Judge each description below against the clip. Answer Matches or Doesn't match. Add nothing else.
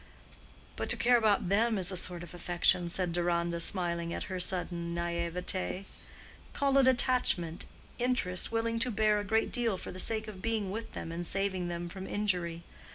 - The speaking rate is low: Doesn't match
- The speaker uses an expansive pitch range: Doesn't match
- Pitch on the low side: Doesn't match